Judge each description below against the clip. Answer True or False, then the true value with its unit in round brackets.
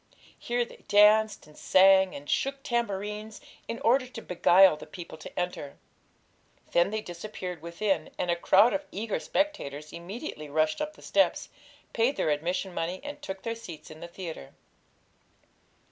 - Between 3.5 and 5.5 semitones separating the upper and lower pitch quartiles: True (5.1 semitones)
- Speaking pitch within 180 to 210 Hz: True (190 Hz)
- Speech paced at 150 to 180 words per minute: True (160 wpm)